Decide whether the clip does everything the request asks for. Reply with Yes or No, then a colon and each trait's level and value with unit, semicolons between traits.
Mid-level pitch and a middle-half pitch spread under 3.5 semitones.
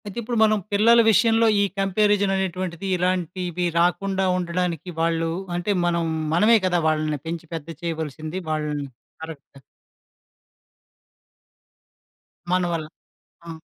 Yes: medium, 175 Hz; average, 3.0 semitones